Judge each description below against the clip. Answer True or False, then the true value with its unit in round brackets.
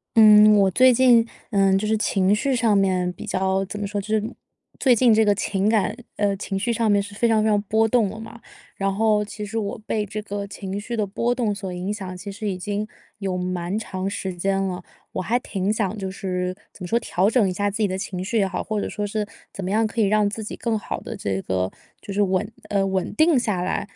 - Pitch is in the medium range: False (205 Hz)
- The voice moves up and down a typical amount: False (2.3 semitones)